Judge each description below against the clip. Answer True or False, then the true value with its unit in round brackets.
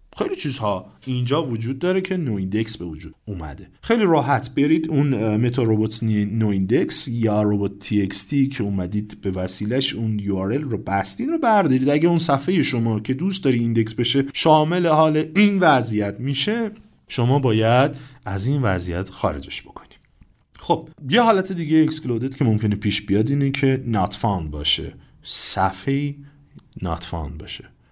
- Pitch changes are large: True (6.2 semitones)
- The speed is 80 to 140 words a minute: False (150 wpm)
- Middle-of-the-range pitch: False (125 Hz)